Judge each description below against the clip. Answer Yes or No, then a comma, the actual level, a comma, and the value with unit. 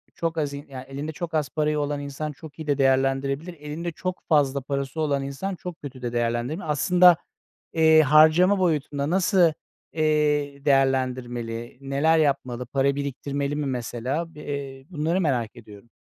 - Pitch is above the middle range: No, medium, 145 Hz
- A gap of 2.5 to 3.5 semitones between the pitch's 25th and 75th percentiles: Yes, average, 2.8 semitones